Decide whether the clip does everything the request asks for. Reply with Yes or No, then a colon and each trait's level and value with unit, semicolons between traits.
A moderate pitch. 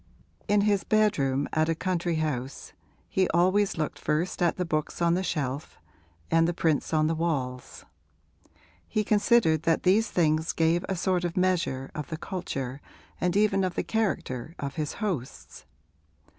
Yes: medium, 165 Hz